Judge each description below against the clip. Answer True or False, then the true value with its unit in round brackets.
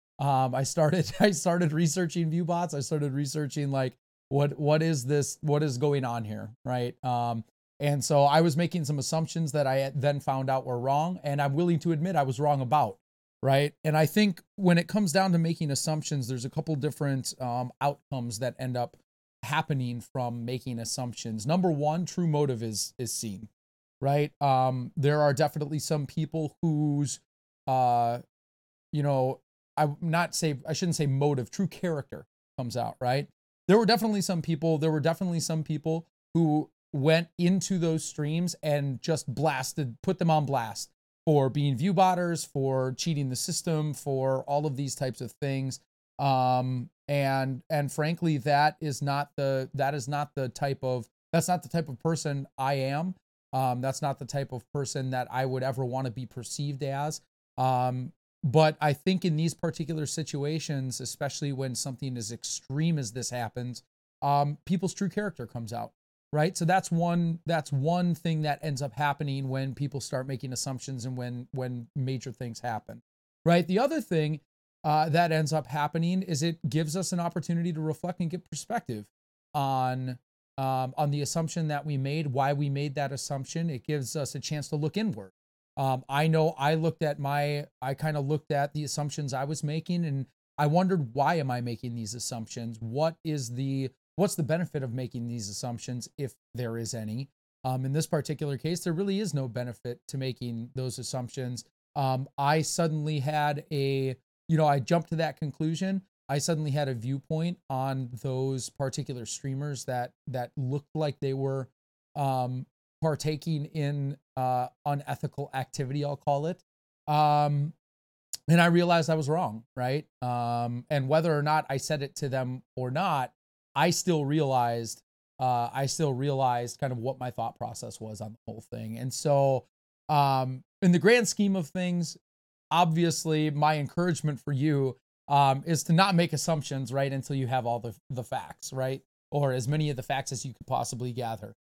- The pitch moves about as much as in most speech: True (3.5 semitones)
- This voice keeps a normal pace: True (180 wpm)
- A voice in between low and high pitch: True (145 Hz)